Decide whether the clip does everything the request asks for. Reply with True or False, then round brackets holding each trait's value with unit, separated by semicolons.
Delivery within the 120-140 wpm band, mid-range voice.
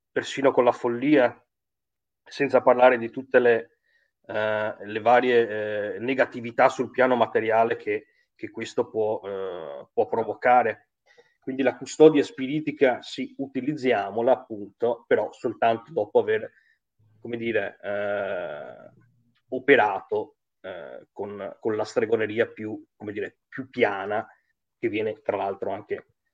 False (125 wpm; 125 Hz)